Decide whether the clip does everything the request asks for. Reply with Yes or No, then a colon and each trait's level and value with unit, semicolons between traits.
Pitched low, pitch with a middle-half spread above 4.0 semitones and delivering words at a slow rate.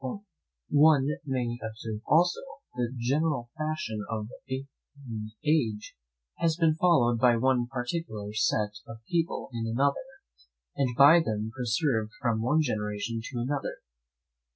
Yes: low, 125 Hz; average, 4.6 semitones; slow, 130 wpm